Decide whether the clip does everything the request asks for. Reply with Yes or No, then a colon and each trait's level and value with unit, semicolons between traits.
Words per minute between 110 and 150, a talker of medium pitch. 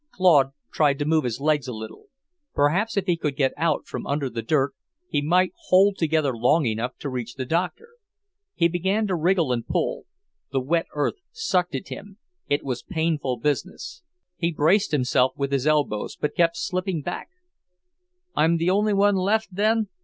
No: average, 180 wpm; medium, 160 Hz